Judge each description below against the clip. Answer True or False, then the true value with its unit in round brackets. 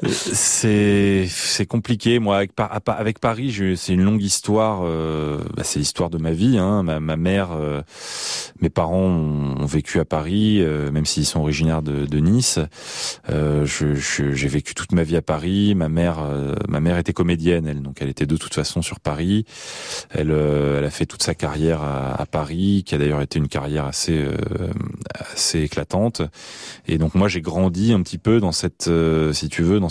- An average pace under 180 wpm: False (200 wpm)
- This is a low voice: True (80 Hz)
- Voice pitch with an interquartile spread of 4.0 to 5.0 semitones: True (4.5 semitones)